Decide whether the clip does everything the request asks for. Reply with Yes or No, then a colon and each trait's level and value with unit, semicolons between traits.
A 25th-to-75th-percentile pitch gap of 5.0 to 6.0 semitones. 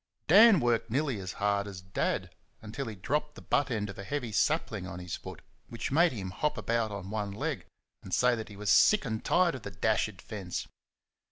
Yes: average, 5.3 semitones